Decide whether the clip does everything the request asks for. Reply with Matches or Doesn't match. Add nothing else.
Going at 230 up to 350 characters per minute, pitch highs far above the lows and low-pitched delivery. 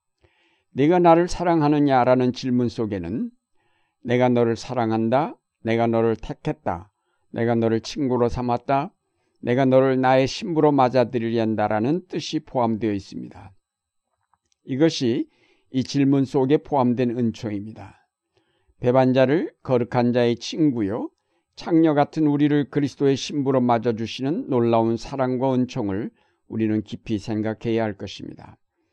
Doesn't match